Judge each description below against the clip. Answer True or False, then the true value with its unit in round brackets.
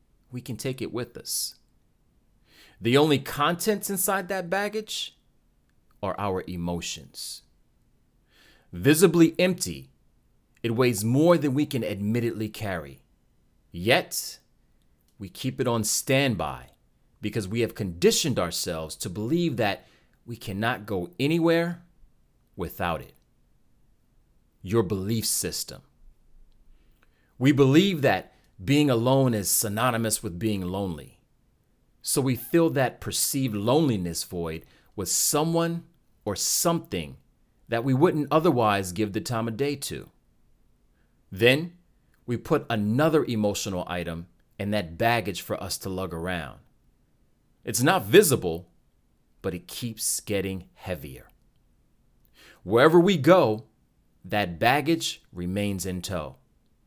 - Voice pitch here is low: True (115 Hz)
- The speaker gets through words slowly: True (115 wpm)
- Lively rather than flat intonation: True (7.6 semitones)